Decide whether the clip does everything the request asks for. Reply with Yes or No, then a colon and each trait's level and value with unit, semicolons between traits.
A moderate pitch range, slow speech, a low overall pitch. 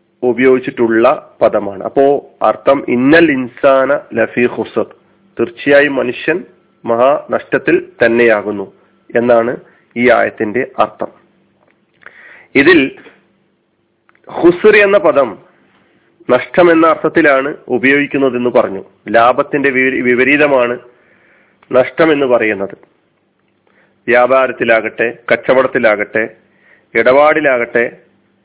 No: average, 3.5 semitones; average, 70 wpm; low, 130 Hz